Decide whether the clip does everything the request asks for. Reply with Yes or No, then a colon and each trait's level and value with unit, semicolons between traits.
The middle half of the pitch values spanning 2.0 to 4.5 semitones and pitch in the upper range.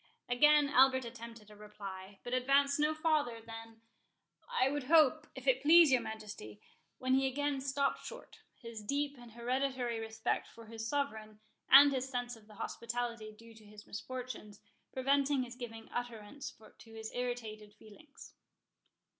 Yes: average, 3.8 semitones; high, 245 Hz